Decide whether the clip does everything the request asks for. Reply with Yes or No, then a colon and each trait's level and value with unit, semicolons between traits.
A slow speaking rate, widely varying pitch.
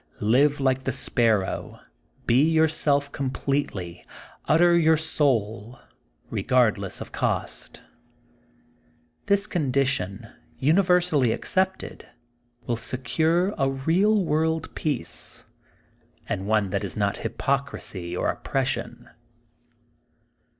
Yes: slow, 100 wpm; wide, 6.0 semitones